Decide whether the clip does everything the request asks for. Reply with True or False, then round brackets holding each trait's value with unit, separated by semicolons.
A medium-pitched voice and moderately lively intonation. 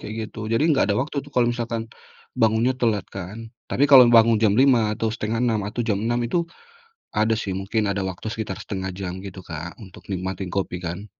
False (110 Hz; 3.2 semitones)